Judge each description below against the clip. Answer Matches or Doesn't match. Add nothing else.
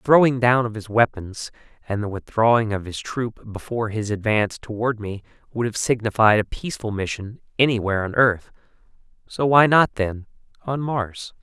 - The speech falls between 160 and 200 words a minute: Matches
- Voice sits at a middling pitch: Doesn't match